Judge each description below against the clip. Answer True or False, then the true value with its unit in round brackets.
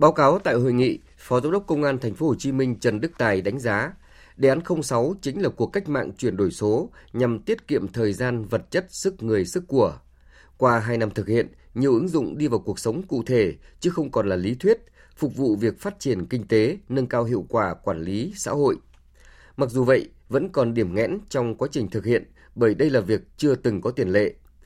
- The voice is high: False (125 Hz)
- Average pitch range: True (4.3 semitones)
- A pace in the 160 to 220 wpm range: False (240 wpm)